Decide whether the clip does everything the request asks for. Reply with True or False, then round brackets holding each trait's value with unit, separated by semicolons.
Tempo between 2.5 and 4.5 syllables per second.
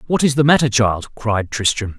False (4.9 syllables/s)